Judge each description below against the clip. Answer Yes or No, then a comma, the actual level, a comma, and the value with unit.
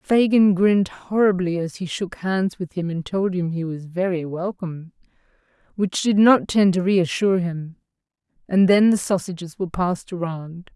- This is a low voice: No, medium, 185 Hz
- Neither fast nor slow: Yes, average, 165 wpm